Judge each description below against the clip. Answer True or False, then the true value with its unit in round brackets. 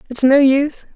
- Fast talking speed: False (190 wpm)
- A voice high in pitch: True (270 Hz)